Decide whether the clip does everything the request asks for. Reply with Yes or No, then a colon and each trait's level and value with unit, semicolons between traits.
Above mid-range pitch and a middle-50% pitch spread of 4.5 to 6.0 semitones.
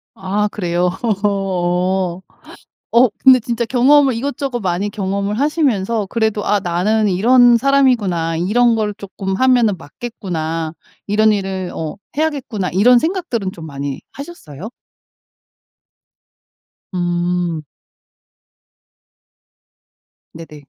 Yes: high, 205 Hz; average, 5.3 semitones